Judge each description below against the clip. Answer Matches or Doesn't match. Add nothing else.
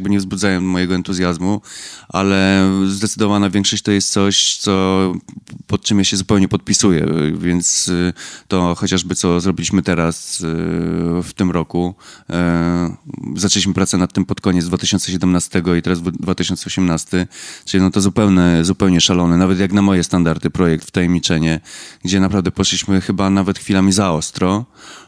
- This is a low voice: Matches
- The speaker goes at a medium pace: Matches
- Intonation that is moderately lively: Doesn't match